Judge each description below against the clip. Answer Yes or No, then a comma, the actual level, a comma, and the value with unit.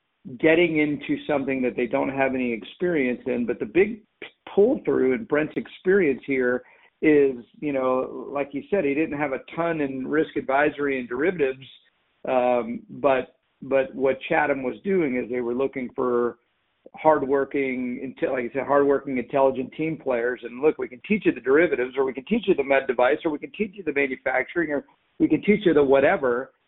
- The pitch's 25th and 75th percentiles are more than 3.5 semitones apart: No, average, 3.2 semitones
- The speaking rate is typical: Yes, average, 190 wpm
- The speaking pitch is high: No, medium, 140 Hz